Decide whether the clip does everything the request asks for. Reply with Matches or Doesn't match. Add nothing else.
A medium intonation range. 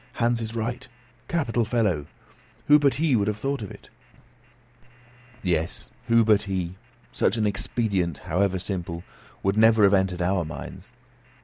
Matches